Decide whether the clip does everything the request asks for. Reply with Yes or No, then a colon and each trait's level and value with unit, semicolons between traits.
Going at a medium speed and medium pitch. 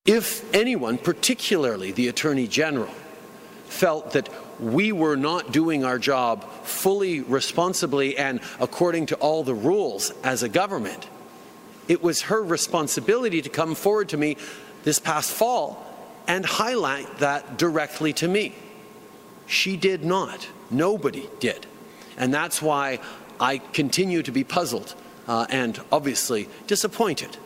No: slow, 130 wpm; medium, 155 Hz